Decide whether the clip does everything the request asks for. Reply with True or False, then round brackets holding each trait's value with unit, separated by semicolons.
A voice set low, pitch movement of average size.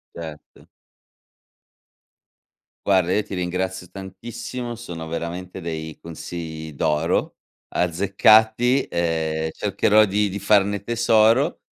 True (95 Hz; 4.5 semitones)